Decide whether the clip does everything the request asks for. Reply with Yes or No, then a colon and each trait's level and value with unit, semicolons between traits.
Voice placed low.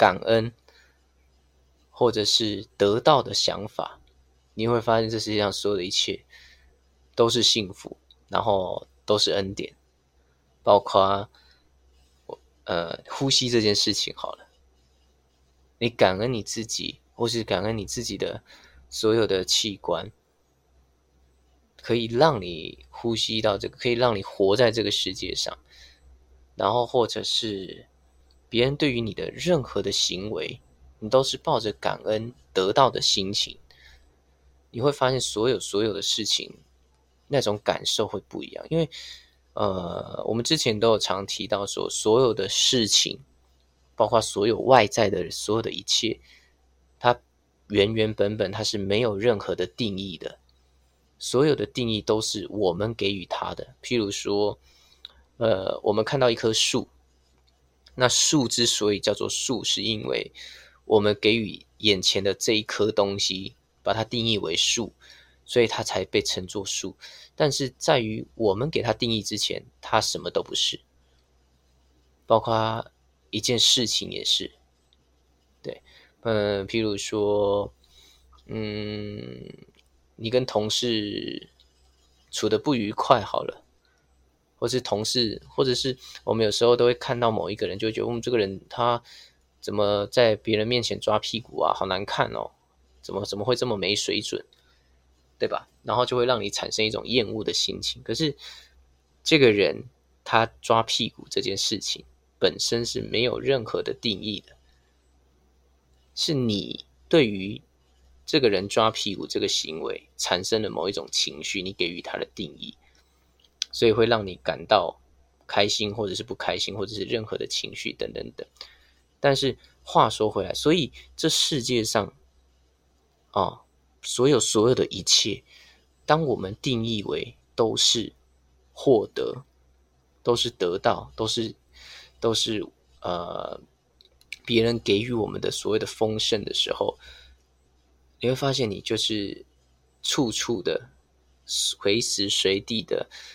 Yes: very low, 95 Hz